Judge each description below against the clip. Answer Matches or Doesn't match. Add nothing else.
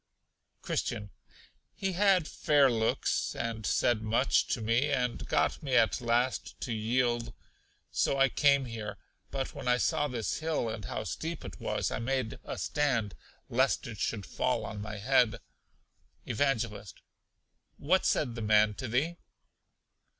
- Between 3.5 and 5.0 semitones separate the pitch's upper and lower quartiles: Matches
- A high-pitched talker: Doesn't match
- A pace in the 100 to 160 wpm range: Matches